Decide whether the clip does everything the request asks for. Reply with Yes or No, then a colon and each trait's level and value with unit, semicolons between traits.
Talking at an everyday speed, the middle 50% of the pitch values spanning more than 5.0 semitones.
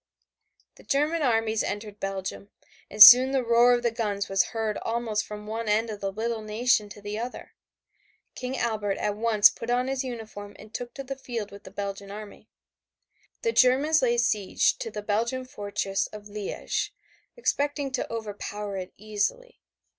No: average, 170 wpm; average, 3.2 semitones